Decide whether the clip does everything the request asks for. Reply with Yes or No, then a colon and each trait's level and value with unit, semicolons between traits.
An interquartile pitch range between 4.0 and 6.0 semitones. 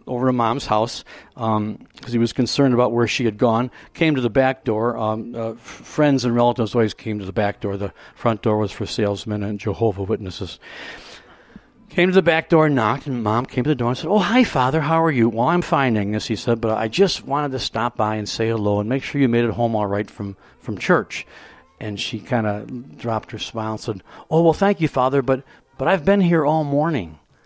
Yes: average, 4.4 semitones